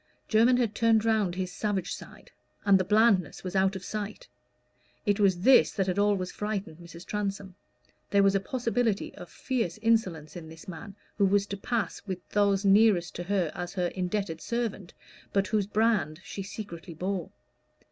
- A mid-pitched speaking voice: No, high, 195 Hz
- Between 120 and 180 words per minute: Yes, average, 175 wpm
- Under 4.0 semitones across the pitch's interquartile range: Yes, average, 2.8 semitones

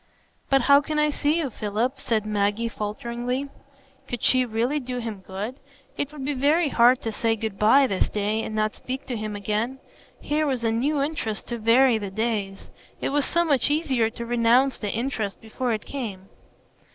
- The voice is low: No, high, 235 Hz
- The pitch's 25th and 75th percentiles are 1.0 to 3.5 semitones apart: No, average, 4.1 semitones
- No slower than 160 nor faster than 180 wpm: No, average, 190 wpm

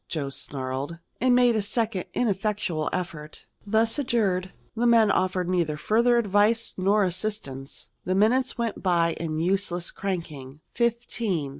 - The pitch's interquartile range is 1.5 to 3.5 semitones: No, average, 5.1 semitones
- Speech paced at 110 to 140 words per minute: Yes, slow, 135 wpm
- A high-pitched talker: Yes, high, 195 Hz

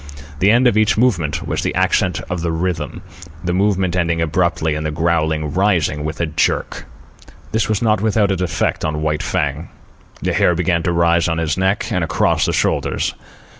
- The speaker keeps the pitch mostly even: No, average, 3.2 semitones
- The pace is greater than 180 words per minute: Yes, average, 190 wpm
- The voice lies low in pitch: Yes, very low, 85 Hz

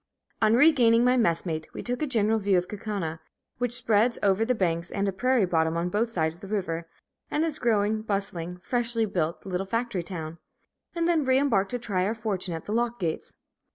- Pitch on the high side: Yes, high, 210 Hz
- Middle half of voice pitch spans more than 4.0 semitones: Yes, average, 5.0 semitones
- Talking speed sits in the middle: No, fast, 210 wpm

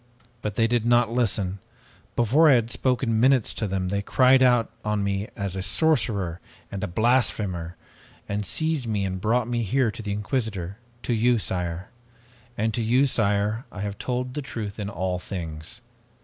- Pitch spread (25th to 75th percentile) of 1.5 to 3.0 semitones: No, average, 3.7 semitones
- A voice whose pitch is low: Yes, low, 110 Hz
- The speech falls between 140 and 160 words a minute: No, average, 175 wpm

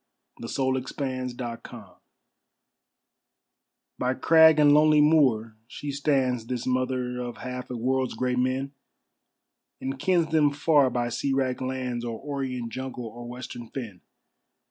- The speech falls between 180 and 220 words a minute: No, slow, 135 wpm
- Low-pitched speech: Yes, low, 130 Hz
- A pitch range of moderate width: No, narrow, 2.2 semitones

